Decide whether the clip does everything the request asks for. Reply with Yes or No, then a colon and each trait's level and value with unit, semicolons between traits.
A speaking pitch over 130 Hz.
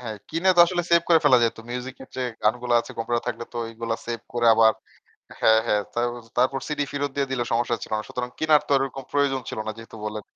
No: low, 125 Hz